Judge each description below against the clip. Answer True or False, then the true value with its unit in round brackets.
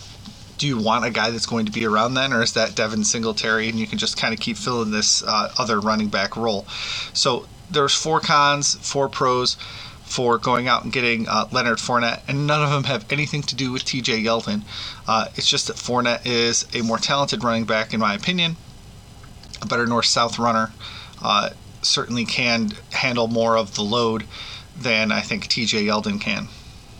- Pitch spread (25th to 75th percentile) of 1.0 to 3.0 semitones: True (2.4 semitones)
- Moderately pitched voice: False (115 Hz)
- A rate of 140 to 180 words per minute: False (195 wpm)